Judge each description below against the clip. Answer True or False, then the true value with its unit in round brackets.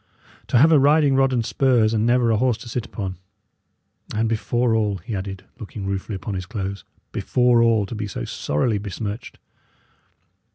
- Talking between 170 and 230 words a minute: True (175 wpm)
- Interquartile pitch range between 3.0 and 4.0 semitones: True (3.5 semitones)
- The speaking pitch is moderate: False (110 Hz)